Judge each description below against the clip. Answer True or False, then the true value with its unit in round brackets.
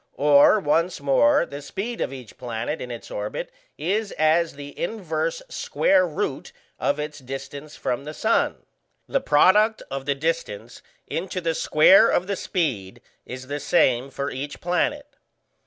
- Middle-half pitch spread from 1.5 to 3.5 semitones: False (5.2 semitones)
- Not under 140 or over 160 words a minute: True (155 wpm)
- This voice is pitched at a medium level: True (150 Hz)